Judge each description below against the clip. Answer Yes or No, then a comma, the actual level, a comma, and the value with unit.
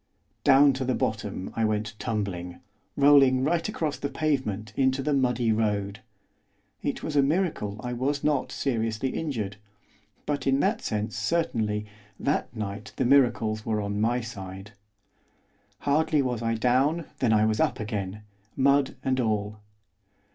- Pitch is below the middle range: Yes, low, 120 Hz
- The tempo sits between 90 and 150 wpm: Yes, average, 145 wpm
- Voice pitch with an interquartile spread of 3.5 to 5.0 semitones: Yes, average, 4.6 semitones